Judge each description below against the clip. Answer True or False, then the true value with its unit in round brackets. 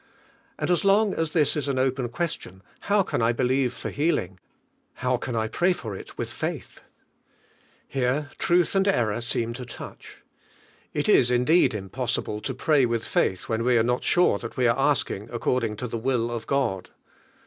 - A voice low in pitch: True (125 Hz)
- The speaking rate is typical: True (180 wpm)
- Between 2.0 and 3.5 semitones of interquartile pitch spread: False (4.1 semitones)